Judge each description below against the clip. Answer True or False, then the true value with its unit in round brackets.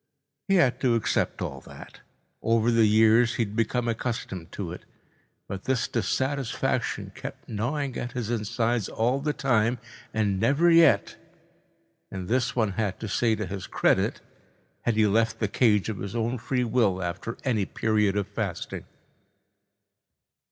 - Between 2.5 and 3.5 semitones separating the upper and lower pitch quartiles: True (2.9 semitones)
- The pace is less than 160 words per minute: True (150 wpm)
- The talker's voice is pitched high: False (115 Hz)